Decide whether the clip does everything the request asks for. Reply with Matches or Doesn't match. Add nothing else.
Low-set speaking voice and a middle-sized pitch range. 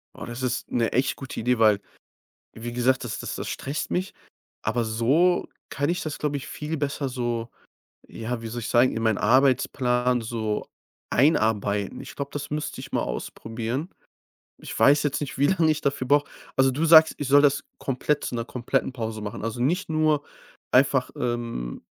Matches